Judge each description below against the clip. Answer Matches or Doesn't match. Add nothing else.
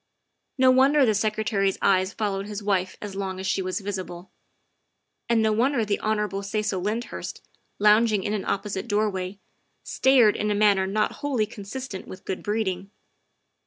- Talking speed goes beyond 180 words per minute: Doesn't match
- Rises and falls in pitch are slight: Matches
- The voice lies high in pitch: Matches